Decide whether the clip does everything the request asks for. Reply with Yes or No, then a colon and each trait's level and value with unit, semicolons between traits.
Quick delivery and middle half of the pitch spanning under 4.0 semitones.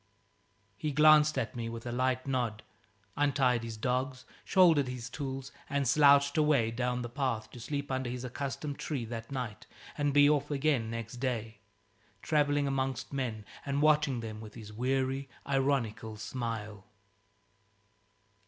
No: average, 145 wpm; average, 3.5 semitones